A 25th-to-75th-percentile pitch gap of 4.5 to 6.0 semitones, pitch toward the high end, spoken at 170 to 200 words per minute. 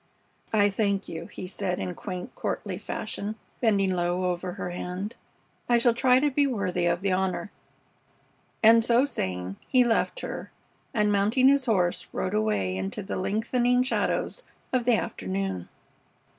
No: average, 4.8 semitones; high, 200 Hz; average, 155 wpm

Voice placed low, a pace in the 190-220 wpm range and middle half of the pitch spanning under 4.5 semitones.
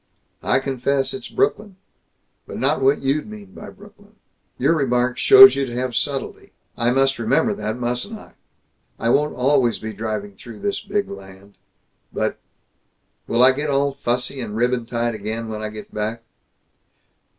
No: low, 125 Hz; average, 160 wpm; average, 4.1 semitones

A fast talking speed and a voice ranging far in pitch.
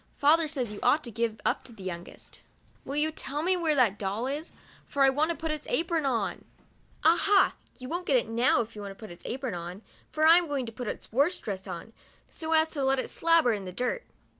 Yes: fast, 265 wpm; wide, 6.2 semitones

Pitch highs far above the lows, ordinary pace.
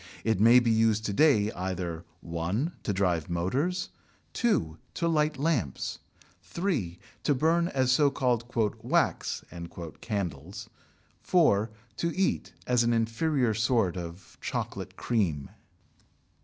No: wide, 7.6 semitones; slow, 120 wpm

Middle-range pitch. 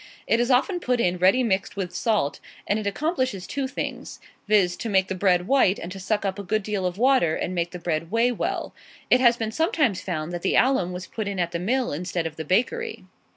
No: high, 200 Hz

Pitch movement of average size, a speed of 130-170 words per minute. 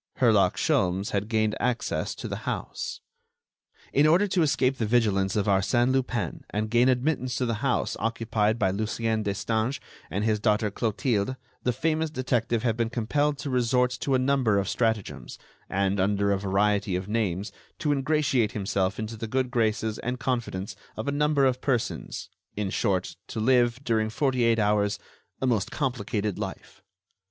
Yes: average, 3.6 semitones; average, 165 wpm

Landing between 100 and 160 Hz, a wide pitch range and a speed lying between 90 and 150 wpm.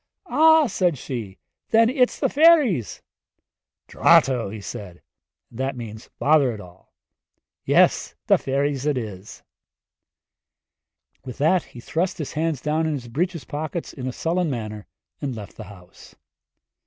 Yes: low, 135 Hz; wide, 6.7 semitones; average, 140 wpm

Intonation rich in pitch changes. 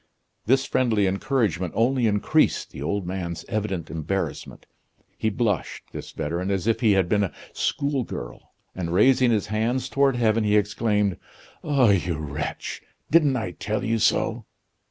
No: average, 4.5 semitones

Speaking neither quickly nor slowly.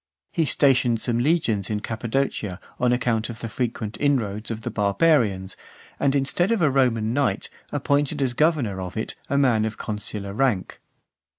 Yes: average, 165 wpm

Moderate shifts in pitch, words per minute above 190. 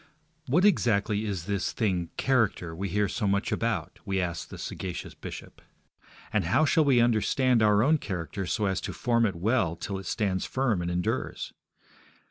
No: average, 4.2 semitones; average, 175 wpm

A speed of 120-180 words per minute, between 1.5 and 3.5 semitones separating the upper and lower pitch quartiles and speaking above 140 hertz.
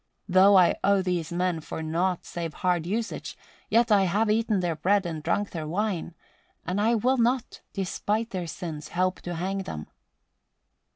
Yes: average, 170 wpm; average, 3.2 semitones; medium, 185 Hz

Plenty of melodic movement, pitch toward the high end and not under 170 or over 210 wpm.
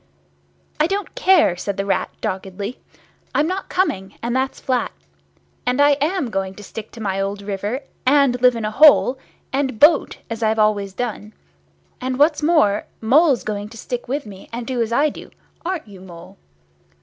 Yes: wide, 5.9 semitones; high, 235 Hz; average, 180 wpm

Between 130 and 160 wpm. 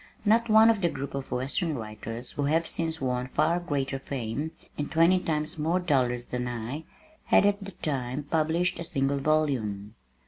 No: average, 175 wpm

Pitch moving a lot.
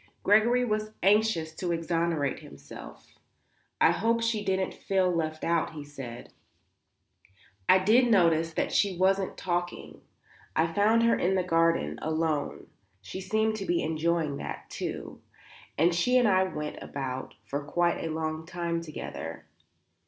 No: average, 3.9 semitones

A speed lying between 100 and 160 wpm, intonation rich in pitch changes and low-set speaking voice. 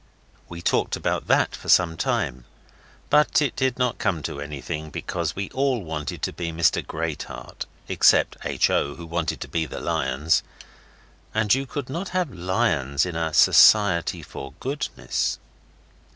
Yes: average, 155 wpm; wide, 7.8 semitones; very low, 85 Hz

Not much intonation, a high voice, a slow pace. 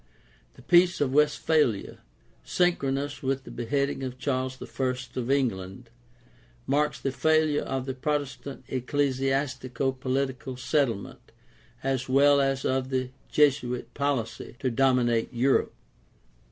No: narrow, 1.8 semitones; low, 135 Hz; slow, 120 wpm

